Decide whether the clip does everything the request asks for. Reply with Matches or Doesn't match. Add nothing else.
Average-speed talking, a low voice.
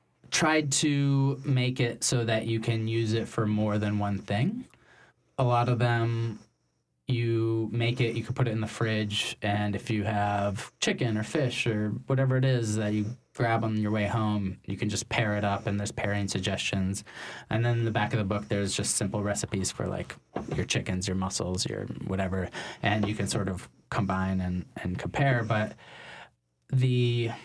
Matches